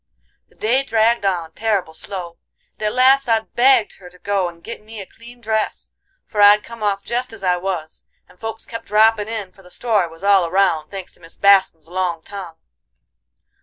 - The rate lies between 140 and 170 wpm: No, average, 200 wpm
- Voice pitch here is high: Yes, high, 200 Hz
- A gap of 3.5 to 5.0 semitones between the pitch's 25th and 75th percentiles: Yes, average, 3.8 semitones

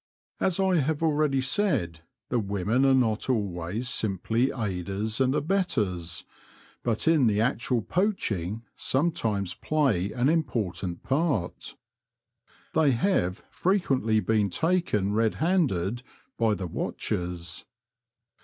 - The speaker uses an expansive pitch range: Yes, wide, 7.2 semitones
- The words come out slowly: Yes, slow, 110 wpm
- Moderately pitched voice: No, low, 115 Hz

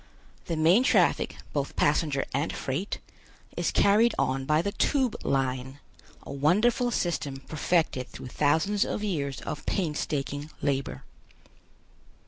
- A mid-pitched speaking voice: Yes, medium, 150 Hz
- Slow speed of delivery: Yes, slow, 120 wpm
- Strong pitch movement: Yes, wide, 5.7 semitones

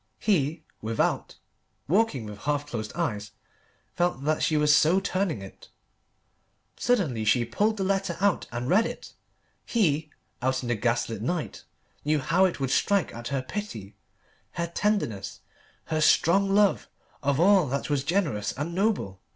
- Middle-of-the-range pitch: Yes, medium, 150 Hz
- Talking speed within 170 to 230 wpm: No, average, 155 wpm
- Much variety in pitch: Yes, wide, 7.8 semitones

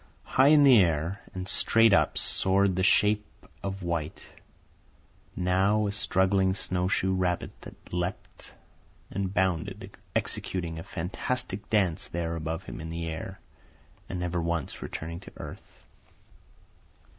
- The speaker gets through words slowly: Yes, slow, 130 wpm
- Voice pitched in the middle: No, very low, 95 Hz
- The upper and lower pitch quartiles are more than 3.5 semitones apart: No, average, 2.7 semitones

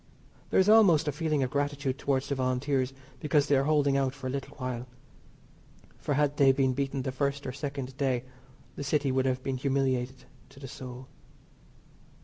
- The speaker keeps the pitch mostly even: Yes, narrow, 1.7 semitones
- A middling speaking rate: Yes, average, 185 wpm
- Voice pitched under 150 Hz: Yes, low, 135 Hz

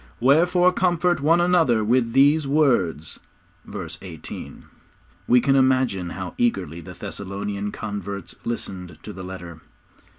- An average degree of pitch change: No, wide, 7.3 semitones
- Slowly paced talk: Yes, slow, 125 wpm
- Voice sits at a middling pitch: No, low, 115 Hz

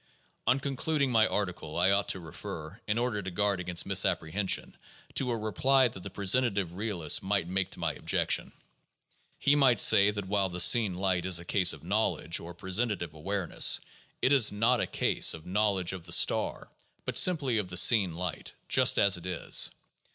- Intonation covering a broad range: No, average, 3.8 semitones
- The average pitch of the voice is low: Yes, low, 100 Hz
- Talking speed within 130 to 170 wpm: No, average, 185 wpm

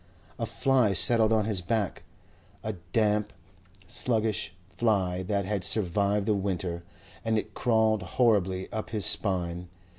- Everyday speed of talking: No, slow, 130 wpm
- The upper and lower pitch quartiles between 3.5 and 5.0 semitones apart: No, average, 2.9 semitones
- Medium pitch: No, low, 105 Hz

